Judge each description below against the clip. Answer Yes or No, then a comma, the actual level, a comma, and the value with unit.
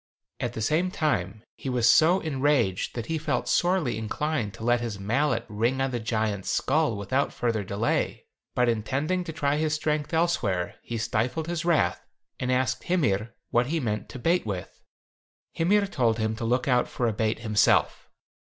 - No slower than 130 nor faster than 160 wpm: No, average, 175 wpm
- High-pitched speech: No, low, 125 Hz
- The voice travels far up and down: Yes, wide, 5.7 semitones